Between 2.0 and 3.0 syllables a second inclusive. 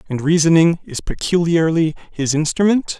No: 5.0 syllables/s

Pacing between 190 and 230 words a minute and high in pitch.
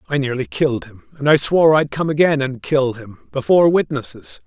No: average, 200 wpm; medium, 140 Hz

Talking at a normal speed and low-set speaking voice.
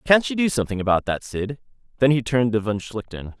No: fast, 230 wpm; low, 120 Hz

